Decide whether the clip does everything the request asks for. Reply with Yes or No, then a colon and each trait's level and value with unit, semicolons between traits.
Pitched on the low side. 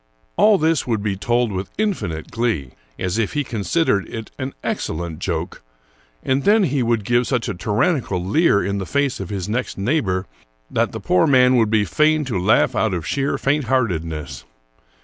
Yes: low, 115 Hz